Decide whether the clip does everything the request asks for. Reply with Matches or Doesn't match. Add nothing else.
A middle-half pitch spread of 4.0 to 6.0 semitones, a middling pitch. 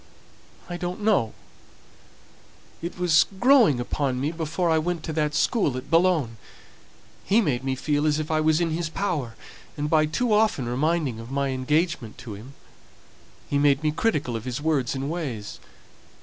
Matches